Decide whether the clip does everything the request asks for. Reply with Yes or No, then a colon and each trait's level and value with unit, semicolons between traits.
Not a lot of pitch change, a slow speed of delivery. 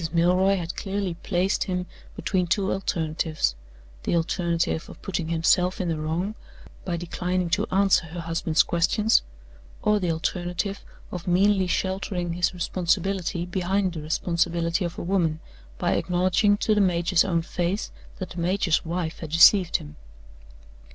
No: narrow, 2.2 semitones; average, 145 wpm